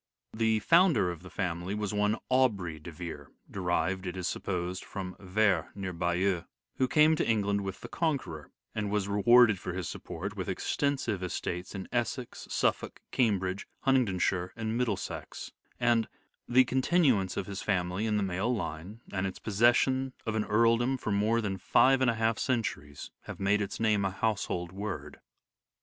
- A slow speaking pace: No, average, 175 wpm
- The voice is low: Yes, low, 100 Hz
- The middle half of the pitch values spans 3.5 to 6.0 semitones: Yes, average, 4.0 semitones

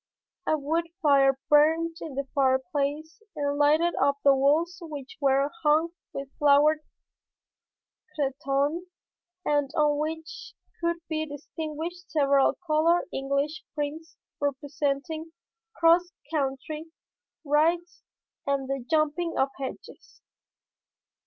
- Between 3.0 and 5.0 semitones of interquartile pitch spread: No, narrow, 2.5 semitones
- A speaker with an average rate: No, slow, 105 wpm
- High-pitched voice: Yes, very high, 295 Hz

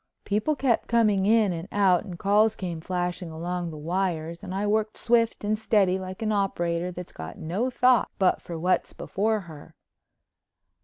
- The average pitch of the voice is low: No, high, 190 Hz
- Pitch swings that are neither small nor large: Yes, average, 3.6 semitones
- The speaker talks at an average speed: Yes, average, 170 wpm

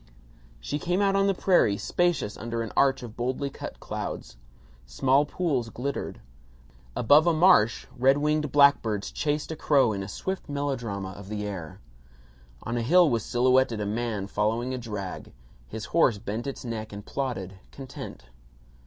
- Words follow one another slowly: No, average, 160 wpm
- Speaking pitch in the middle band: No, low, 120 Hz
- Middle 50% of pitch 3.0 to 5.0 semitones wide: No, wide, 5.4 semitones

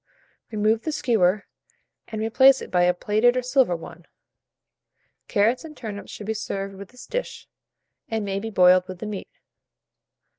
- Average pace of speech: Yes, average, 160 wpm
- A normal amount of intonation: Yes, average, 4.0 semitones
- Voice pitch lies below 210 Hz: No, high, 215 Hz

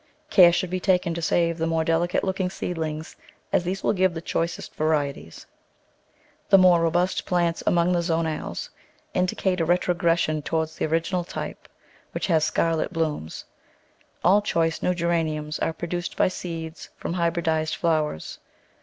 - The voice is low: No, medium, 170 Hz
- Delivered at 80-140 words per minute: No, average, 155 wpm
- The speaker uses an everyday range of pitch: No, narrow, 1.8 semitones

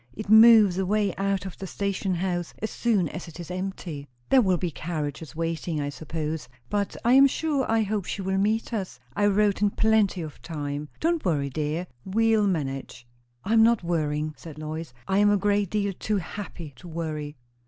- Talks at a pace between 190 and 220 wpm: Yes, average, 195 wpm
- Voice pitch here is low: No, medium, 185 Hz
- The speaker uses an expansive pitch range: No, average, 4.6 semitones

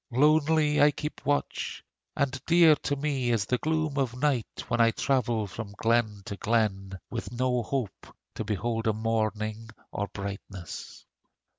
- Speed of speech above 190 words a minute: No, average, 150 wpm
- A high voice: No, low, 120 Hz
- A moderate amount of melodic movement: Yes, average, 4.7 semitones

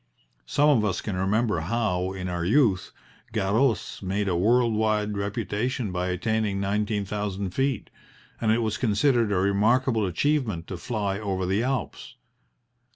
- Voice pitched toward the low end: Yes, low, 105 Hz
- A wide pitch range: No, average, 3.2 semitones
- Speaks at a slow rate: No, average, 150 wpm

